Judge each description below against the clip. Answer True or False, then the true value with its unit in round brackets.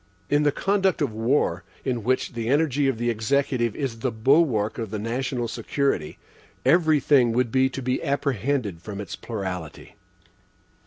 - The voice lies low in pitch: True (125 Hz)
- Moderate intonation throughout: True (4.1 semitones)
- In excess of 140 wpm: True (160 wpm)